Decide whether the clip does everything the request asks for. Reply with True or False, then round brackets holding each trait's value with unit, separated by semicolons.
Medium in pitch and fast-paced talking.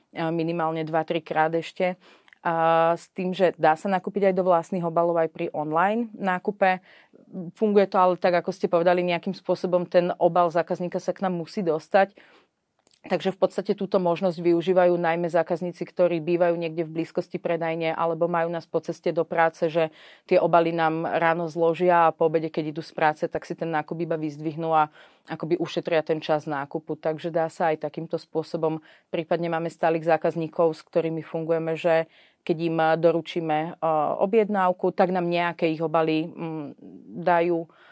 True (170 Hz; 170 wpm)